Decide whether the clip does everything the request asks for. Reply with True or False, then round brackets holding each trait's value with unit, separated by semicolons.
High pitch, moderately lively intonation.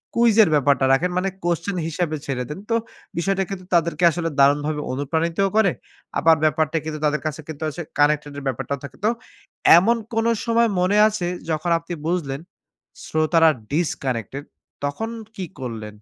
False (160 Hz; 4.0 semitones)